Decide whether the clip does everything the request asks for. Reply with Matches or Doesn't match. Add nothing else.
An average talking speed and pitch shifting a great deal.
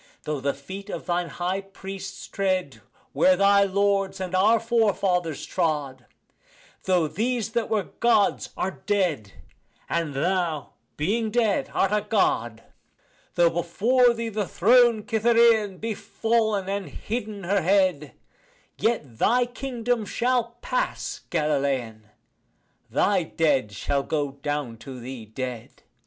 Doesn't match